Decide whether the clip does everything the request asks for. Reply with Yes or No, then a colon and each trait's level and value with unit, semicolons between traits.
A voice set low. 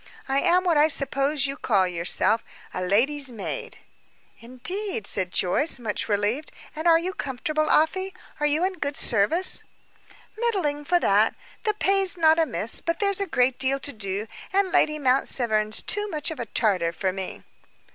No: very high, 285 Hz